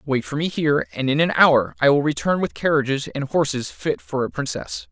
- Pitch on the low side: No, medium, 145 Hz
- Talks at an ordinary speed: No, fast, 230 wpm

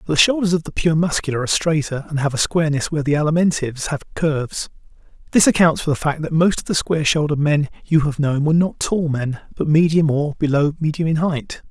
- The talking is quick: Yes, fast, 225 wpm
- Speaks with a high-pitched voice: No, medium, 155 Hz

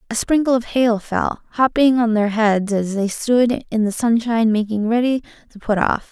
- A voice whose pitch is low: No, high, 230 Hz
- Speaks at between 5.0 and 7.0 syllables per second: No, 4.8 syllables/s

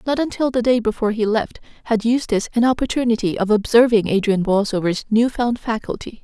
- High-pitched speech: Yes, high, 225 Hz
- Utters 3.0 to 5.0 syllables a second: No, 6.0 syllables/s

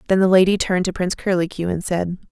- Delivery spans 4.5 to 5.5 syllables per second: No, 7.0 syllables/s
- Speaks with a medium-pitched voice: Yes, medium, 180 Hz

